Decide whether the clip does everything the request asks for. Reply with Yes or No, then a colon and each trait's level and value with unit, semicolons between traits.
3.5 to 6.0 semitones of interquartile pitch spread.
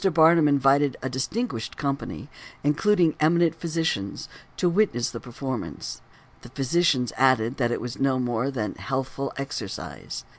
Yes: average, 4.5 semitones